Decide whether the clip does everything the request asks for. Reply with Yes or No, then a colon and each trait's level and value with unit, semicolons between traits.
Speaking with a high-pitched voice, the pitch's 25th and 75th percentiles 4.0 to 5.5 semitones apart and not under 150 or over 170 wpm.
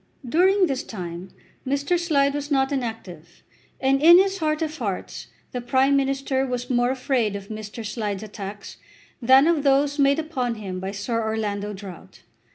Yes: very high, 255 Hz; average, 5.2 semitones; average, 165 wpm